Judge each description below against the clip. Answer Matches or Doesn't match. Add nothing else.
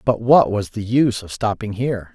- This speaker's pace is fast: Matches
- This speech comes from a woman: Doesn't match